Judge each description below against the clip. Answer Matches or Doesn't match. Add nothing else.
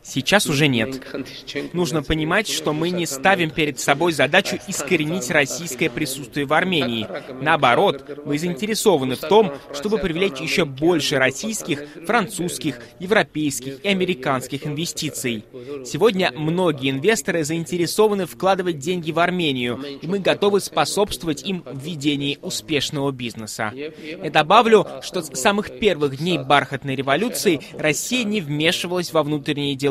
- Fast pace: Doesn't match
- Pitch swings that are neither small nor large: Matches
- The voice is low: Doesn't match